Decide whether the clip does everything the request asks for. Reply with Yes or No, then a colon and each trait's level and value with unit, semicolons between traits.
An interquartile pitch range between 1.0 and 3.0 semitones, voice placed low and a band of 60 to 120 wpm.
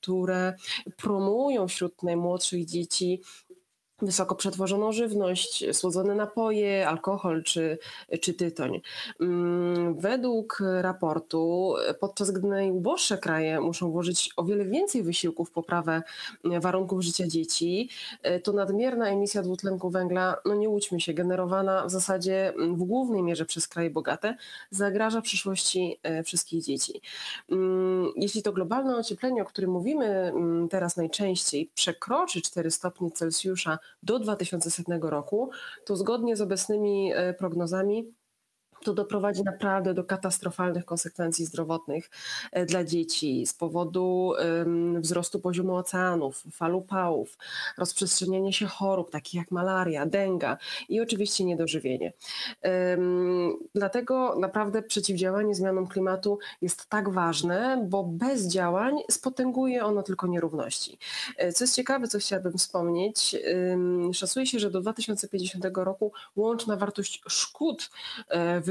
No: average, 2.7 semitones; medium, 185 Hz; average, 115 wpm